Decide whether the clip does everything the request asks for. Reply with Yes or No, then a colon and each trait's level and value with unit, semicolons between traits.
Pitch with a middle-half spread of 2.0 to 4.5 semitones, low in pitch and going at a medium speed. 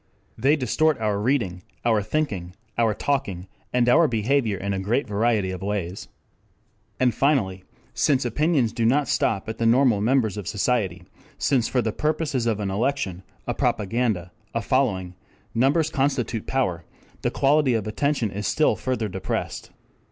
No: average, 5.1 semitones; low, 115 Hz; average, 155 wpm